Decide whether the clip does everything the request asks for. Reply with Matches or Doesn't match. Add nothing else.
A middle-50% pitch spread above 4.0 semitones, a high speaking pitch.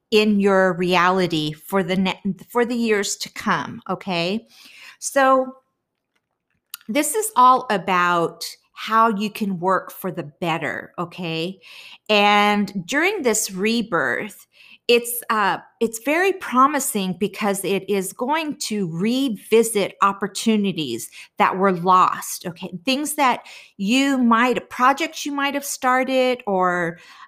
Matches